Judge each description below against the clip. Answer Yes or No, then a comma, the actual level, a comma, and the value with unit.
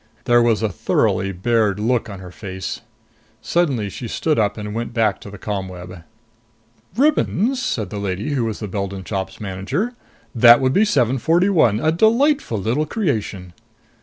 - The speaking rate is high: No, average, 160 wpm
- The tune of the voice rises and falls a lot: Yes, wide, 7.2 semitones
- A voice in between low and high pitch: No, low, 110 Hz